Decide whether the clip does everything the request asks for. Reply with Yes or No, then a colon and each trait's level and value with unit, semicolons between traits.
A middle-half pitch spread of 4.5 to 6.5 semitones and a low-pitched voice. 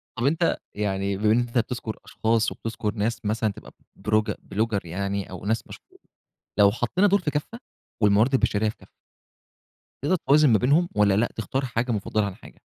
No: average, 3.4 semitones; low, 110 Hz